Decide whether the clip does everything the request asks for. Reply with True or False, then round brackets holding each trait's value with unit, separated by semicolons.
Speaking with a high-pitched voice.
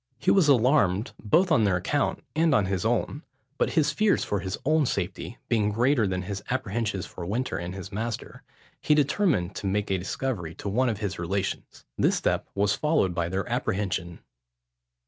False (105 Hz)